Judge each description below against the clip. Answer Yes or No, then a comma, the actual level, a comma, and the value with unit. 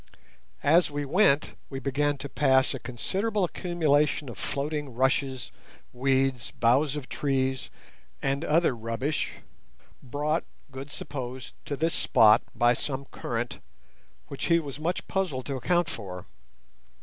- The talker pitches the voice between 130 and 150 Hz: Yes, medium, 140 Hz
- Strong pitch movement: No, average, 2.7 semitones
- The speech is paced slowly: Yes, slow, 130 wpm